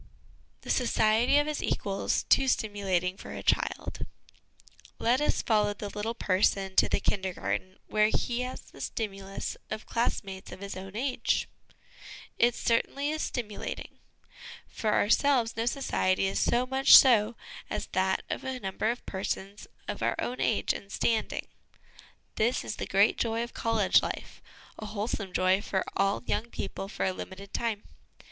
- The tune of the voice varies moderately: Yes, average, 3.5 semitones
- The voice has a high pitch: Yes, high, 215 Hz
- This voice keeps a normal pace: Yes, average, 160 wpm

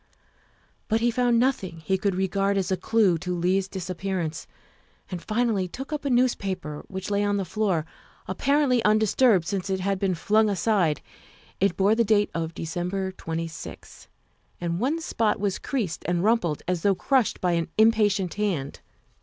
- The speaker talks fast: No, average, 165 wpm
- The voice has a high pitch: Yes, high, 195 Hz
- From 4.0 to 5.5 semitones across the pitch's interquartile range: No, average, 3.6 semitones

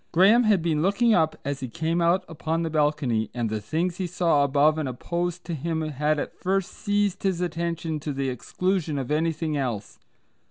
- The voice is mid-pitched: Yes, medium, 160 Hz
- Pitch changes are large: No, average, 3.4 semitones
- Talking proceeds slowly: No, average, 195 wpm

